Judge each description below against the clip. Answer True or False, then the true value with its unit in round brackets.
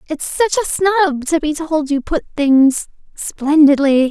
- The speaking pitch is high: True (305 Hz)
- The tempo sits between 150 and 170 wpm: True (160 wpm)